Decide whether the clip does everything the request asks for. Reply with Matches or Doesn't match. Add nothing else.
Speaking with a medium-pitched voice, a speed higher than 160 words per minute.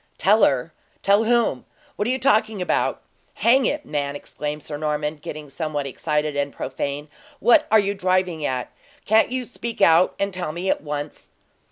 Matches